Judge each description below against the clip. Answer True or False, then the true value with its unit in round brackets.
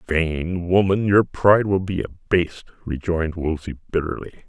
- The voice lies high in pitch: False (85 Hz)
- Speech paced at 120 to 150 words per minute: True (135 wpm)